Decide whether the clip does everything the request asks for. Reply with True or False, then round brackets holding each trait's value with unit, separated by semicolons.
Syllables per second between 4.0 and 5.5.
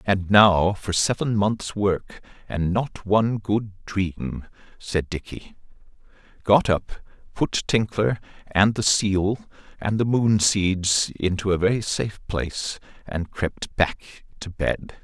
False (3.5 syllables/s)